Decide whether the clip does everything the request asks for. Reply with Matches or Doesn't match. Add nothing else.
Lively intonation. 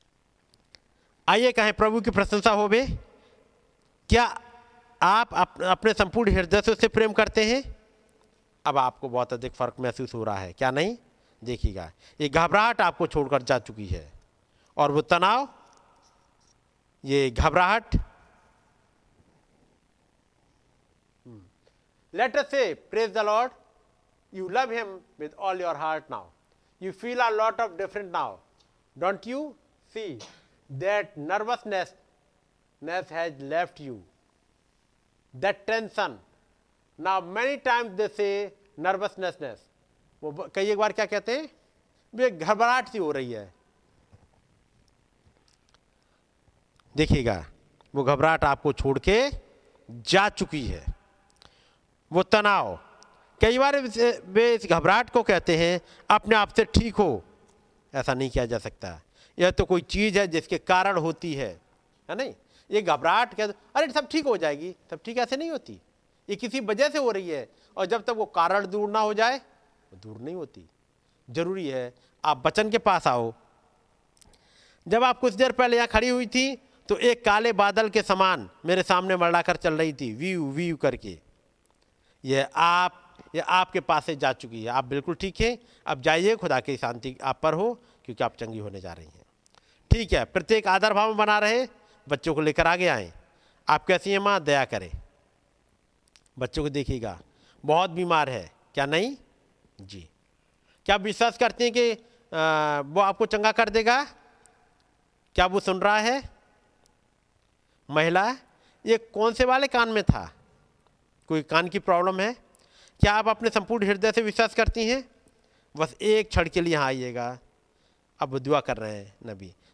Matches